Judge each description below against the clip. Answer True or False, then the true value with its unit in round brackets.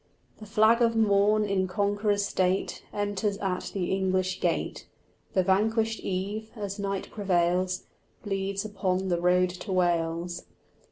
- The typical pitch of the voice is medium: False (195 Hz)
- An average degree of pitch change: False (2.0 semitones)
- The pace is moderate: False (130 wpm)